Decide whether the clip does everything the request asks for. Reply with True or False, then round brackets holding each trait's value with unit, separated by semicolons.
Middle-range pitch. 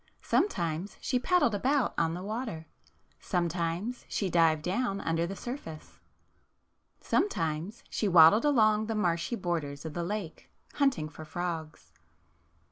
True (180 Hz)